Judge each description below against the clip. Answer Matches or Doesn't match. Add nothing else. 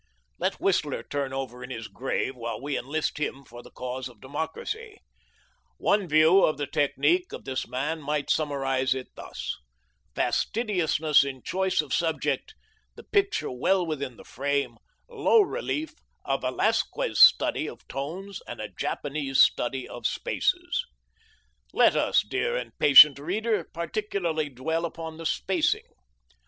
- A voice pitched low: Doesn't match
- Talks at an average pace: Matches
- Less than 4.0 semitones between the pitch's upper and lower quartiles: Doesn't match